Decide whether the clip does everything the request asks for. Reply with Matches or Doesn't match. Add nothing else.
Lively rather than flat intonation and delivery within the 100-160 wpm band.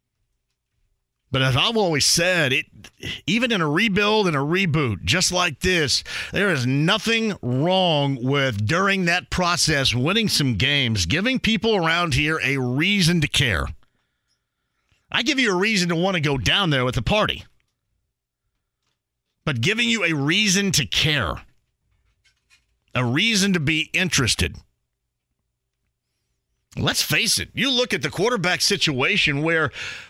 Matches